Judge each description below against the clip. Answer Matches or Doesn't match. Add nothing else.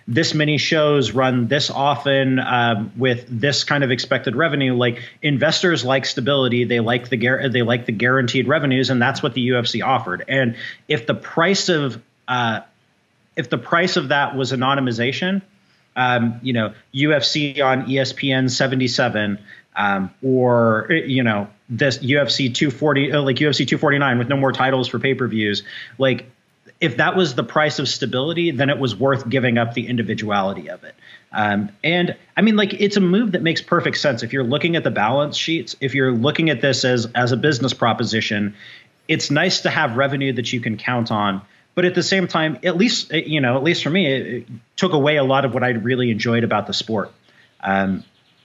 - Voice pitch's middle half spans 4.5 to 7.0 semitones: Doesn't match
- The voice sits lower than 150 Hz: Matches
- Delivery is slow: Doesn't match